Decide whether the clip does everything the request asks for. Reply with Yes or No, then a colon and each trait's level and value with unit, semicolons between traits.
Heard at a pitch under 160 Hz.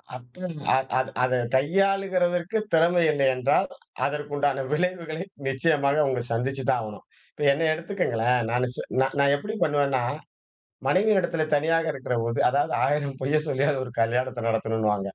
Yes: medium, 140 Hz